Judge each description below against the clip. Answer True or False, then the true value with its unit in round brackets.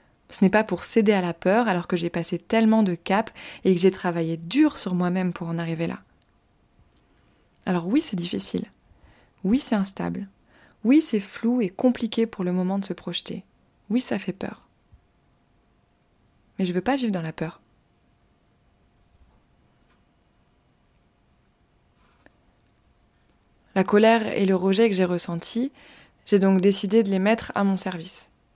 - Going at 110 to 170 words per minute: True (155 wpm)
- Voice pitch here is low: False (195 Hz)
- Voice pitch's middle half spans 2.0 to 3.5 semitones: False (4.0 semitones)